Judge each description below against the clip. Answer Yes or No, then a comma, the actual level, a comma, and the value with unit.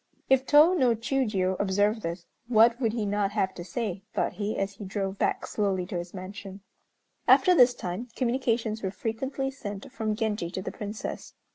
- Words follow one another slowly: No, average, 180 wpm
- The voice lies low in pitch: No, high, 210 Hz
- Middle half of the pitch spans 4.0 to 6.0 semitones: No, average, 3.6 semitones